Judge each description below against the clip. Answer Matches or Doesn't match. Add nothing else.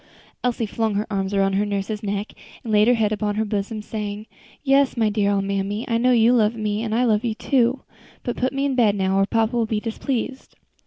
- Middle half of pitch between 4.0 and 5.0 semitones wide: Doesn't match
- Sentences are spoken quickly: Matches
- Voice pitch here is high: Matches